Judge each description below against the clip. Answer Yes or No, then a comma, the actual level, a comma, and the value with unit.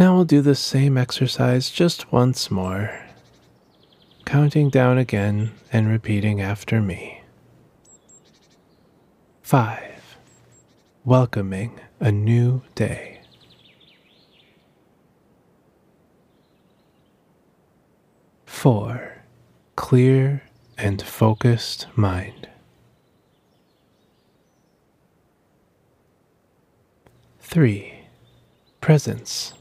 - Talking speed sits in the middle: No, slow, 55 wpm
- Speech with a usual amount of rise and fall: Yes, average, 4.5 semitones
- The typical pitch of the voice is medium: No, low, 115 Hz